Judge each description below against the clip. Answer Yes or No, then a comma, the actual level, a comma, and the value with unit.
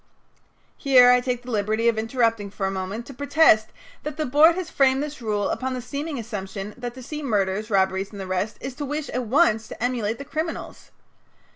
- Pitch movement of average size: Yes, average, 4.9 semitones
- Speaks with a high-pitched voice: Yes, high, 240 Hz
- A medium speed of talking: No, fast, 210 wpm